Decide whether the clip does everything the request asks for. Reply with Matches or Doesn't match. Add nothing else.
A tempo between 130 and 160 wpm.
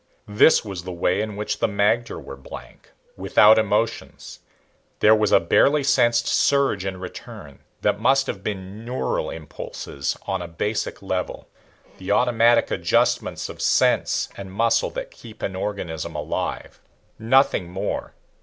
Matches